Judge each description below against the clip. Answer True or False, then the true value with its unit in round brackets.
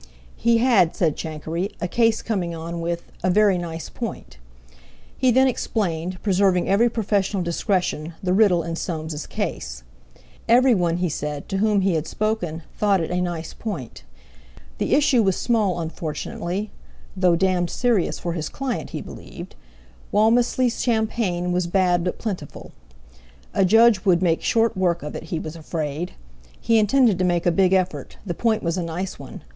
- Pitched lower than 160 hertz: False (180 Hz)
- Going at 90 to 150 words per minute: False (160 wpm)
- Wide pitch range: False (4.3 semitones)